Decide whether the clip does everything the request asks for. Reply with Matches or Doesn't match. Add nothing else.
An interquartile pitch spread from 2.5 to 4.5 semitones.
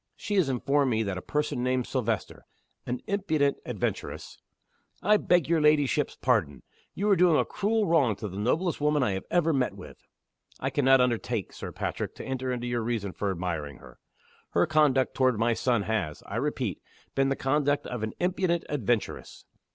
Doesn't match